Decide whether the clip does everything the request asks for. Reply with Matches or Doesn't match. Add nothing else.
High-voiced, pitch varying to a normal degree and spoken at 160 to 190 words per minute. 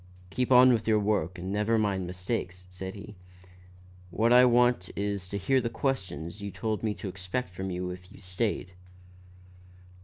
Doesn't match